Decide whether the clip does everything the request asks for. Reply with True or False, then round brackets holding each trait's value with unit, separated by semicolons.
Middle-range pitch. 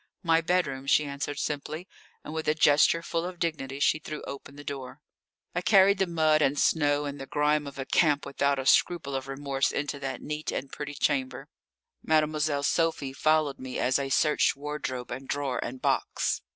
True (145 Hz)